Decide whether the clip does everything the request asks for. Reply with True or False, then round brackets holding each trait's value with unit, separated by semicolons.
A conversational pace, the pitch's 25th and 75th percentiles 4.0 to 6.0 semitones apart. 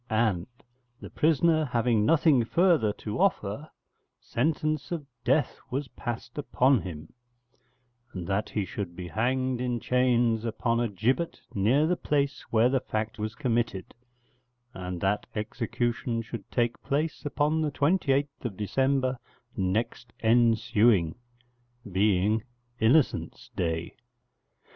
False (120 wpm; 4.7 semitones)